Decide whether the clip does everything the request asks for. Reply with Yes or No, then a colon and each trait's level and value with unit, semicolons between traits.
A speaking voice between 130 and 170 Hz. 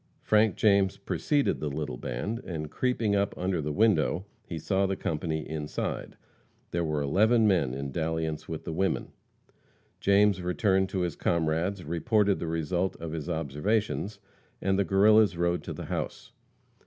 No: very low, 90 Hz